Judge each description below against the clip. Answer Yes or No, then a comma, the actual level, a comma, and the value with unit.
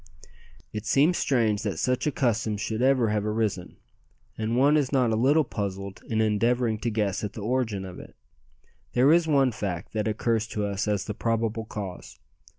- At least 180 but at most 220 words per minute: Yes, average, 185 wpm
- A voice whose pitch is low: Yes, low, 110 Hz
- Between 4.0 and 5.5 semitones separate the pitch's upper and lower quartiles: No, average, 3.2 semitones